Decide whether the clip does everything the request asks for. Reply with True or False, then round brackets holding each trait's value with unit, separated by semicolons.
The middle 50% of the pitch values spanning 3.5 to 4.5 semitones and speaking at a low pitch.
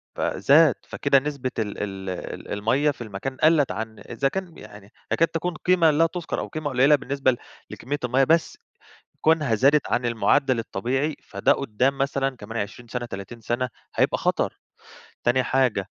True (4.1 semitones; 130 Hz)